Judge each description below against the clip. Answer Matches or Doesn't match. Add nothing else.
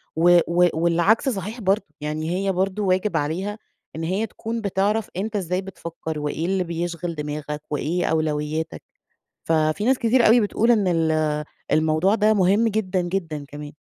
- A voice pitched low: Doesn't match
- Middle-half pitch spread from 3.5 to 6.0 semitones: Matches